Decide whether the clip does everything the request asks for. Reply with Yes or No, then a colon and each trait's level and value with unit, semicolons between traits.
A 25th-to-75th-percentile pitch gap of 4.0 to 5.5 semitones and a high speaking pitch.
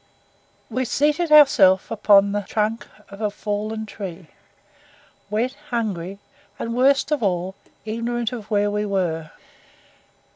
No: average, 3.2 semitones; high, 215 Hz